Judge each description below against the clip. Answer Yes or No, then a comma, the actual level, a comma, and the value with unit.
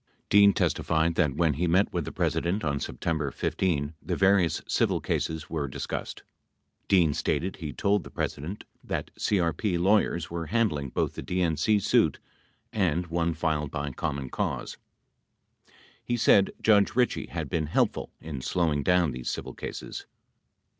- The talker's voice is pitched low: Yes, very low, 85 Hz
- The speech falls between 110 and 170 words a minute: Yes, average, 150 wpm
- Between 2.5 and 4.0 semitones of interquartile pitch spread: No, average, 4.4 semitones